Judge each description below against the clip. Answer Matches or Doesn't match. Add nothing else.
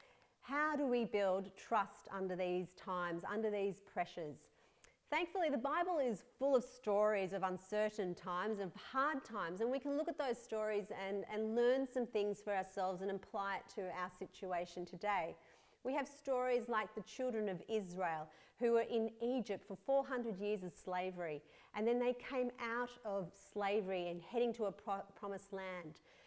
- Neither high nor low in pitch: Doesn't match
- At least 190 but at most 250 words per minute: Doesn't match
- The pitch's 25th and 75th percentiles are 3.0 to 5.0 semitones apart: Matches